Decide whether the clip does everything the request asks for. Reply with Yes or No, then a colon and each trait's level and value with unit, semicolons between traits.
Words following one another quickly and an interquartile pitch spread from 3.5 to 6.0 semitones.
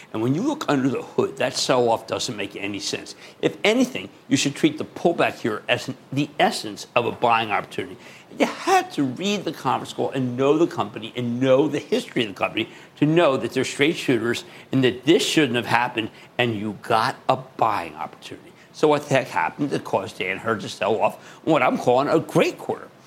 Yes: fast, 215 wpm; wide, 5.4 semitones